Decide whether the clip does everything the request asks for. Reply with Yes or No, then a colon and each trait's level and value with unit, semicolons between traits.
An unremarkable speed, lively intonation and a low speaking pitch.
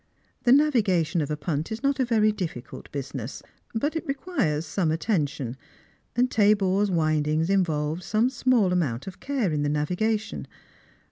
No: average, 150 wpm; wide, 6.7 semitones; medium, 185 Hz